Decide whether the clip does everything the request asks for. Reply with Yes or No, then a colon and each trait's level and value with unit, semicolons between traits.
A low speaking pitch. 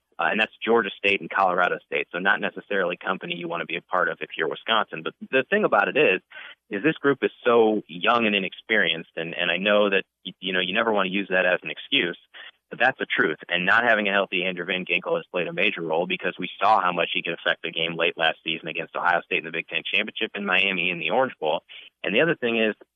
Yes: low, 100 Hz